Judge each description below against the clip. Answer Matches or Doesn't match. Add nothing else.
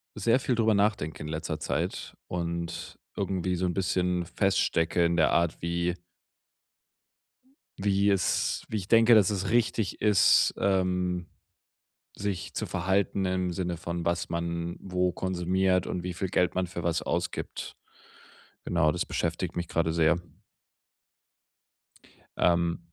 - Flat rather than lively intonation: Matches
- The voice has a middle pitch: Doesn't match